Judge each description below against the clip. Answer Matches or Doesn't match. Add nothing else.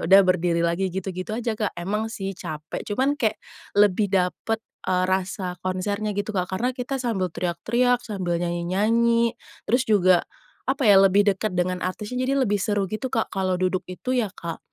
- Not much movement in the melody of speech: Doesn't match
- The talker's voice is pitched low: Doesn't match